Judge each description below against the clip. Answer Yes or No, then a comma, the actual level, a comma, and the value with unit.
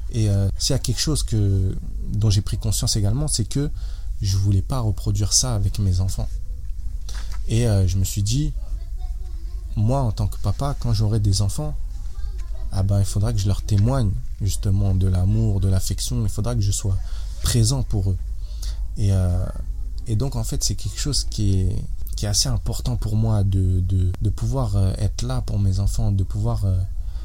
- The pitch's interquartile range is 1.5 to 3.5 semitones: Yes, average, 3.2 semitones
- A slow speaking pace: No, average, 190 wpm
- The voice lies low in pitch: Yes, low, 100 Hz